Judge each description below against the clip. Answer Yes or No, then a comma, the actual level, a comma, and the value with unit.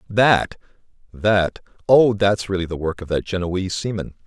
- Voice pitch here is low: Yes, very low, 95 Hz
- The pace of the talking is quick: No, average, 140 wpm